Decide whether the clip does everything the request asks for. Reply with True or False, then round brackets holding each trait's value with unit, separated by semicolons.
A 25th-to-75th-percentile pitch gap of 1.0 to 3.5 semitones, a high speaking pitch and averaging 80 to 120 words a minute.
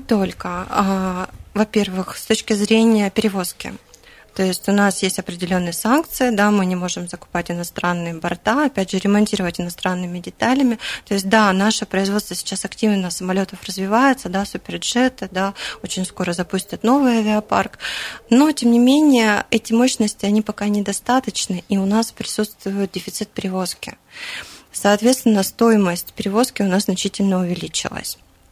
False (2.9 semitones; 200 Hz; 135 wpm)